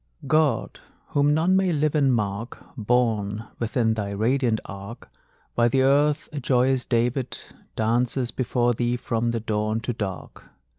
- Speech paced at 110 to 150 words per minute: Yes, average, 145 wpm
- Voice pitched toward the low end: Yes, low, 120 Hz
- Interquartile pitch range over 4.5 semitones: No, average, 3.3 semitones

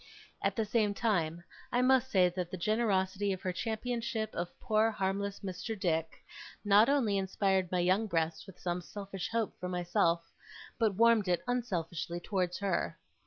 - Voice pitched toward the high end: Yes, high, 195 Hz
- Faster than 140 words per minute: Yes, average, 165 wpm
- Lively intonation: No, average, 3.6 semitones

